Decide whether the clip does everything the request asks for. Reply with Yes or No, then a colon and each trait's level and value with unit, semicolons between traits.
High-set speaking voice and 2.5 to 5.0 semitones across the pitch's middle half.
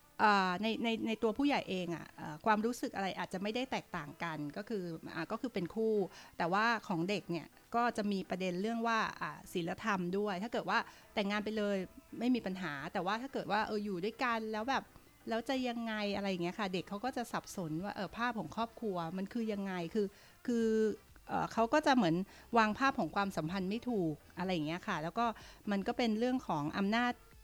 Yes: high, 210 Hz; average, 3.8 semitones